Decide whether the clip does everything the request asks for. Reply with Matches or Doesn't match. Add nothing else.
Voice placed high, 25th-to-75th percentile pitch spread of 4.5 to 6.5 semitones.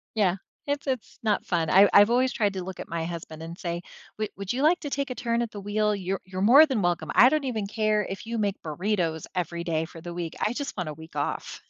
Matches